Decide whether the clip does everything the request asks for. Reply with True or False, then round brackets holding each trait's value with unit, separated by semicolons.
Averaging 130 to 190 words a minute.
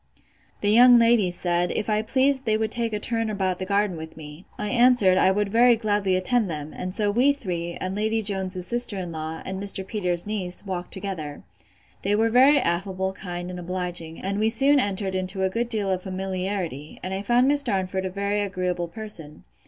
False (205 wpm)